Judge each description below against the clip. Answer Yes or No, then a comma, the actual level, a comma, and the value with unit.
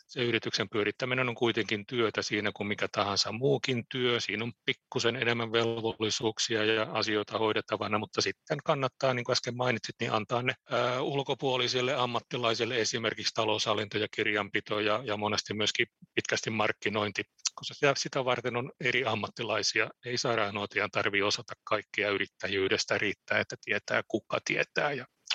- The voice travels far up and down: No, average, 2.9 semitones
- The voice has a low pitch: Yes, low, 115 Hz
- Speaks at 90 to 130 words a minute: No, average, 140 wpm